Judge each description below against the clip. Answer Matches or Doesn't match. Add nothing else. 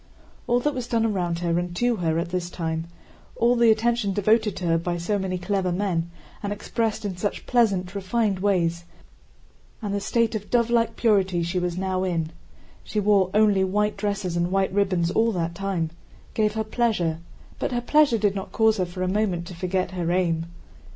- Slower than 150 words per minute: Doesn't match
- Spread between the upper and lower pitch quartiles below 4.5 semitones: Matches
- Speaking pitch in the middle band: Doesn't match